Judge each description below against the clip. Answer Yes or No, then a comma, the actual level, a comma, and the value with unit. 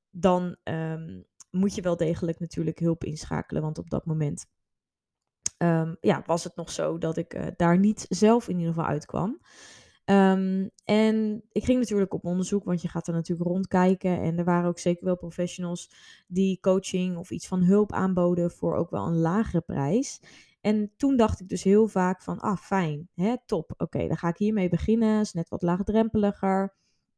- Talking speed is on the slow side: No, average, 190 wpm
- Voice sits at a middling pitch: Yes, medium, 180 Hz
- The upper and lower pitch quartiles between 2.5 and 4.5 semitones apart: Yes, average, 3.0 semitones